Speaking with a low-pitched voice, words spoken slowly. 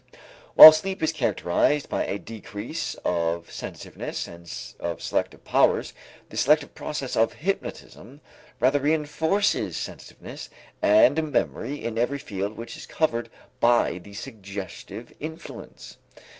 Yes: low, 120 Hz; slow, 120 wpm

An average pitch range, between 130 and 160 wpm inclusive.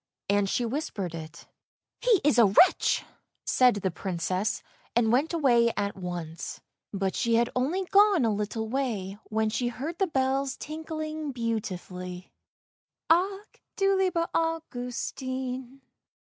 No: wide, 7.4 semitones; average, 140 wpm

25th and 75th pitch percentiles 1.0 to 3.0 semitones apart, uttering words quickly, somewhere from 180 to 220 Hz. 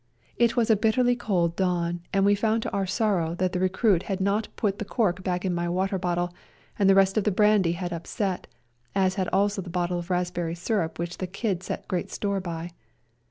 Yes: narrow, 2.6 semitones; fast, 215 wpm; high, 190 Hz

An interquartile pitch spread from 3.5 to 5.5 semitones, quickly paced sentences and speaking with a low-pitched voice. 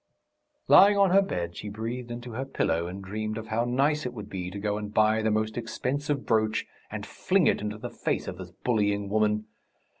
No: average, 2.8 semitones; fast, 210 wpm; low, 110 Hz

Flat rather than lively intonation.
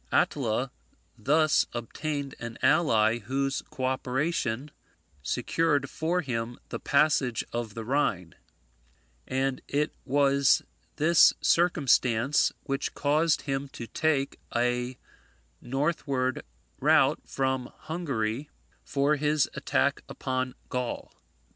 No: average, 3.4 semitones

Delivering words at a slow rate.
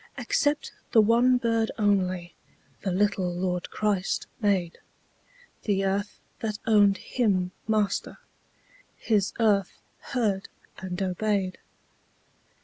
Yes: slow, 100 wpm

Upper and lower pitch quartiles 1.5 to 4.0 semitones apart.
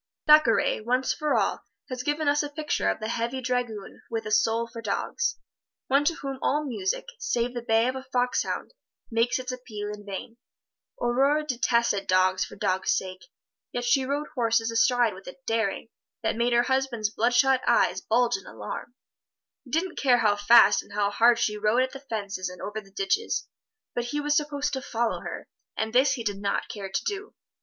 Yes: average, 3.7 semitones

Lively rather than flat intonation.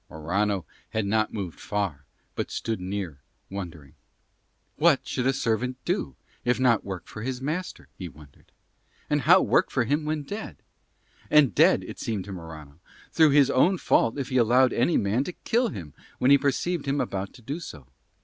Yes: wide, 6.6 semitones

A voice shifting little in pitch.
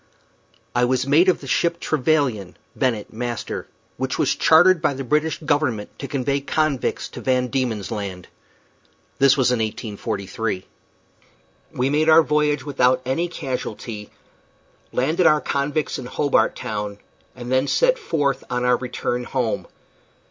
No: average, 3.7 semitones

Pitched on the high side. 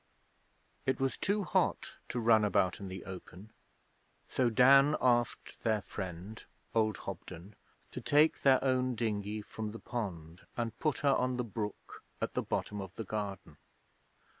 No: low, 110 Hz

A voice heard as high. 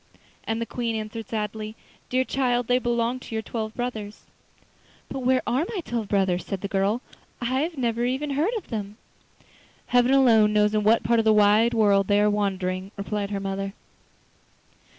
Yes: high, 220 Hz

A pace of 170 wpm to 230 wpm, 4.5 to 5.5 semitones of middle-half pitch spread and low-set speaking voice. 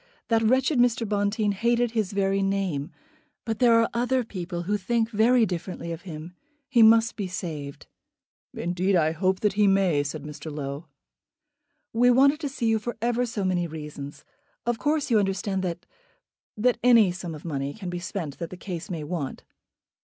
No: average, 175 wpm; average, 5.1 semitones; high, 195 Hz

